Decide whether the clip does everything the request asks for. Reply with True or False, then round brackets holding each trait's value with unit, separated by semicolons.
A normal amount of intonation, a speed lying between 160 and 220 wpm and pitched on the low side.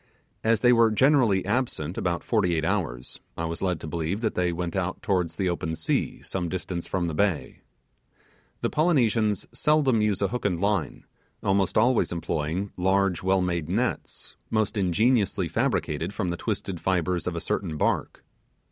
True (4.0 semitones; 170 wpm; 95 Hz)